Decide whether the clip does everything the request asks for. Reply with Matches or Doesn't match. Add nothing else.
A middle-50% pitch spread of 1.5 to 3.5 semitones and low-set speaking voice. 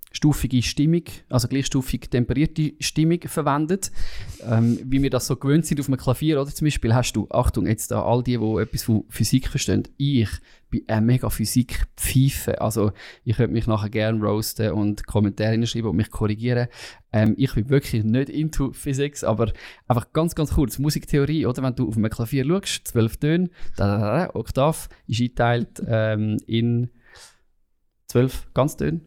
Doesn't match